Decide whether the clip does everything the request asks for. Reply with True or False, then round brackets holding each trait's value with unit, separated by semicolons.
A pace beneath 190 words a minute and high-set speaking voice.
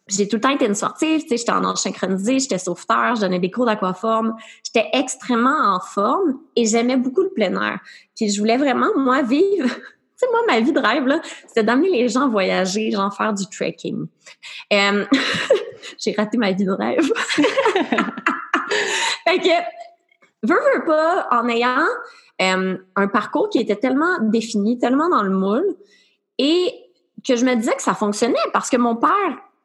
True (180 wpm; 250 Hz)